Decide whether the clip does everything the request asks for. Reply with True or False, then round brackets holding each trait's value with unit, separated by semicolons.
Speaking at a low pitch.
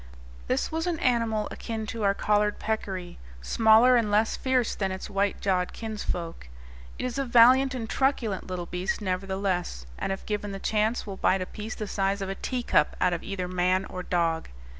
False (205 Hz)